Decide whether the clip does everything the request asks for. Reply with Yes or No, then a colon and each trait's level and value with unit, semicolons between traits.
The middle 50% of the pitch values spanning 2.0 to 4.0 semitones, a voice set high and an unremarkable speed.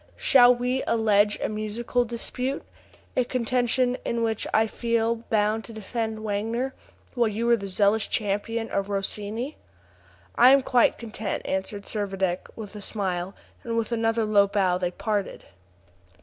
Yes: narrow, 2.6 semitones; high, 220 Hz; average, 150 wpm